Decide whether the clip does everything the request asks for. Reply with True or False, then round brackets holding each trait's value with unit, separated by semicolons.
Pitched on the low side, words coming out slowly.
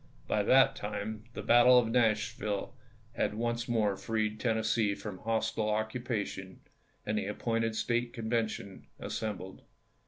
True (110 Hz; 125 wpm)